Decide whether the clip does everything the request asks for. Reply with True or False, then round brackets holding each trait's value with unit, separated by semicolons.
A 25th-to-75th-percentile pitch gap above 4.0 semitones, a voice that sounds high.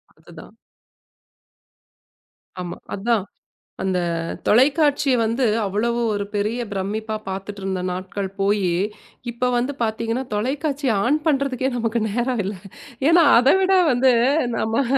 True (4.6 semitones; 230 Hz)